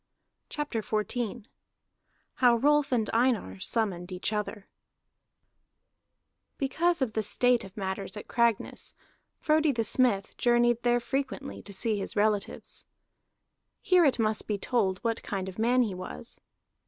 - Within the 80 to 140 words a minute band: Yes, slow, 135 wpm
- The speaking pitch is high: Yes, high, 230 Hz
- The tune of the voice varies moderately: Yes, average, 3.7 semitones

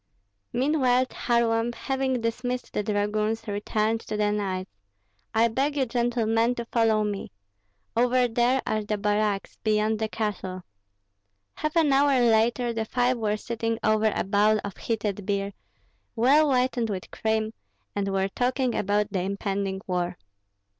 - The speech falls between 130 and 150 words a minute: Yes, average, 145 wpm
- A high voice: Yes, high, 220 Hz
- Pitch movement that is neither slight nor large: Yes, average, 3.0 semitones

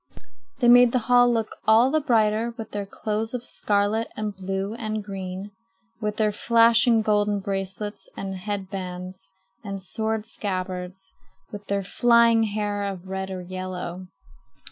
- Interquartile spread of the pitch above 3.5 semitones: No, average, 2.7 semitones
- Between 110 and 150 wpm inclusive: Yes, average, 145 wpm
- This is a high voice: Yes, high, 205 Hz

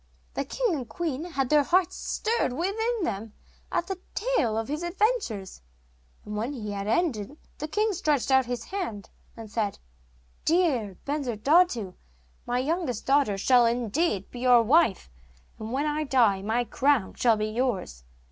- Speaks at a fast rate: No, average, 155 wpm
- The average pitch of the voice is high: Yes, very high, 255 Hz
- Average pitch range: No, wide, 7.2 semitones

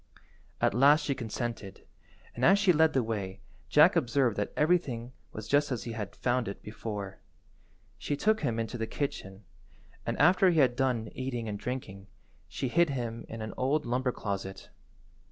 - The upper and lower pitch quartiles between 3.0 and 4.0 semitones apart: No, average, 4.4 semitones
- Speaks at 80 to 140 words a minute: No, average, 170 wpm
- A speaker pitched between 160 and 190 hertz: No, low, 120 Hz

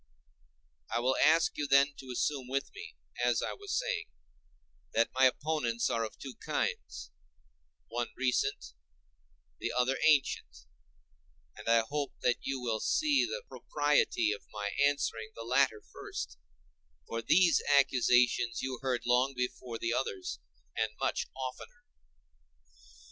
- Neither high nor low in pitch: No, low, 125 Hz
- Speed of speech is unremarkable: No, slow, 130 wpm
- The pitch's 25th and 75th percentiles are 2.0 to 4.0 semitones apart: Yes, average, 3.6 semitones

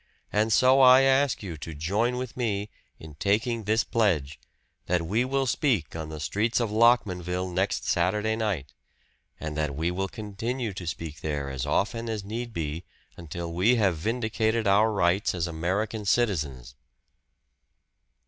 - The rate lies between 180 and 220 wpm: No, average, 155 wpm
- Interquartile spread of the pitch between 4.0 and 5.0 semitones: No, wide, 5.5 semitones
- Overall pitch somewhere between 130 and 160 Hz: No, low, 100 Hz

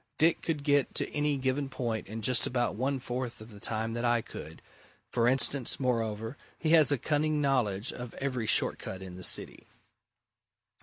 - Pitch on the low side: Yes, low, 125 Hz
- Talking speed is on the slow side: No, average, 185 wpm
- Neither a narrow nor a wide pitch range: Yes, average, 3.8 semitones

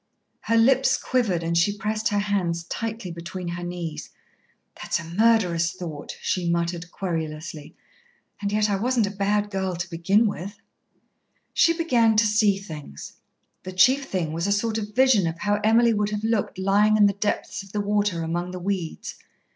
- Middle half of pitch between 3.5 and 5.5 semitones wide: Yes, average, 3.8 semitones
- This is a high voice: Yes, high, 200 Hz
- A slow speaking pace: No, average, 180 wpm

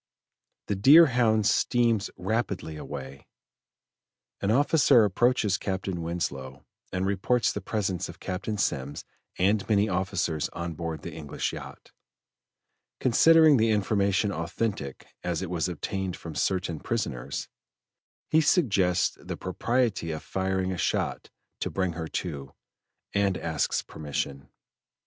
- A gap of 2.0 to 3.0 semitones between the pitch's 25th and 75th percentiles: No, average, 4.7 semitones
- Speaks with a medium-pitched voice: No, very low, 95 Hz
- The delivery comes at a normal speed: No, slow, 120 wpm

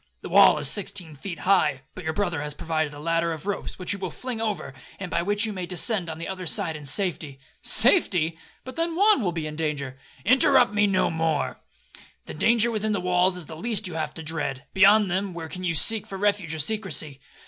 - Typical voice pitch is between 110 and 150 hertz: No, medium, 180 Hz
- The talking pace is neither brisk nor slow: No, fast, 215 wpm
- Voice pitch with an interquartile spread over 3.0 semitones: Yes, average, 4.5 semitones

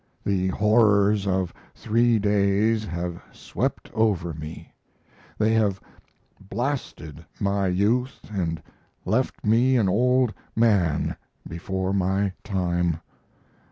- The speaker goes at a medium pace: No, slow, 100 wpm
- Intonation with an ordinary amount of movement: Yes, average, 3.3 semitones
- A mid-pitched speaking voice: No, low, 100 Hz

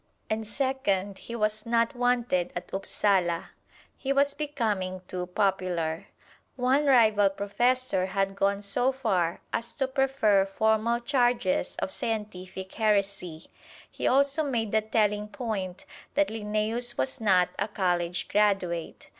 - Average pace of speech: No, slow, 130 wpm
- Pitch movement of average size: Yes, average, 4.1 semitones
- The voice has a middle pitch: No, high, 210 Hz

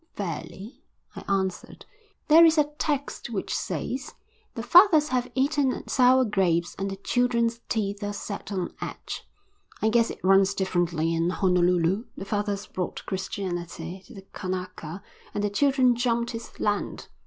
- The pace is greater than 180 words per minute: No, average, 150 wpm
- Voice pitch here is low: No, high, 205 Hz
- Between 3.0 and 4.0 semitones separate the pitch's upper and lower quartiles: No, average, 5.0 semitones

